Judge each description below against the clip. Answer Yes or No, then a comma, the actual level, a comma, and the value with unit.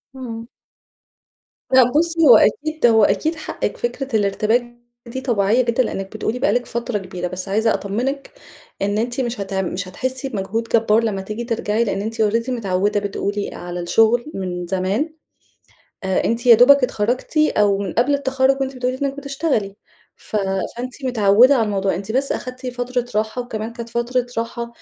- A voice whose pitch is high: Yes, high, 230 Hz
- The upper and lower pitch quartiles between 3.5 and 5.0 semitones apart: Yes, average, 4.0 semitones